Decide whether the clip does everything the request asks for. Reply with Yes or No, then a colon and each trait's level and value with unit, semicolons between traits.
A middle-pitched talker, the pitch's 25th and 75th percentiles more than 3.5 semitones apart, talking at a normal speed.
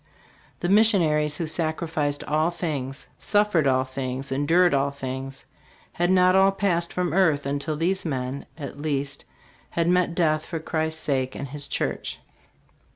Yes: medium, 155 Hz; average, 3.9 semitones; average, 150 wpm